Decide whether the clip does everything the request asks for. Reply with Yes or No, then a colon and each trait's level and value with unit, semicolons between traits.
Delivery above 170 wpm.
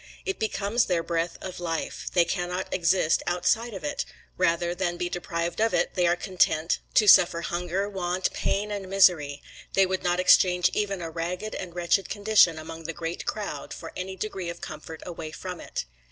Yes: average, 185 wpm